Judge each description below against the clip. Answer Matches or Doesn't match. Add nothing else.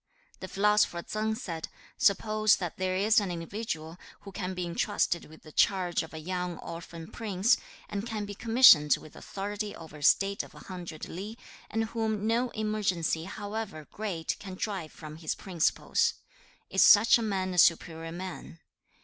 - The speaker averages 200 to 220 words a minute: Doesn't match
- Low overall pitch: Doesn't match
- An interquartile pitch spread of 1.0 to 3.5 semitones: Doesn't match